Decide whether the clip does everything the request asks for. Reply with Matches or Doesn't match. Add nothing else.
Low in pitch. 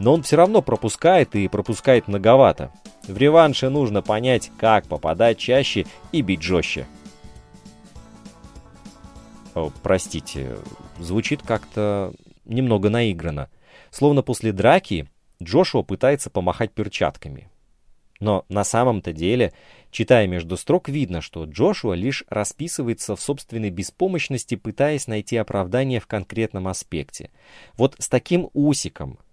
Matches